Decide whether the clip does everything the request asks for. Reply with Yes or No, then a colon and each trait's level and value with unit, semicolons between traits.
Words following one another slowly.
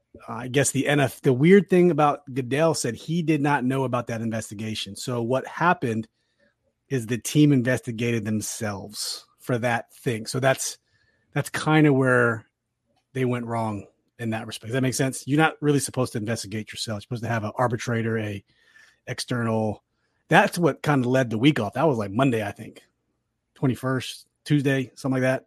No: average, 185 wpm